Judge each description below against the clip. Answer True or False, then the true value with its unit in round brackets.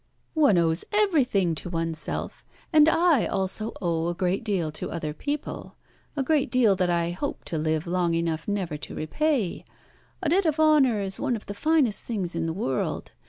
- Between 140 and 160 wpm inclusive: False (185 wpm)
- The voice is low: False (195 Hz)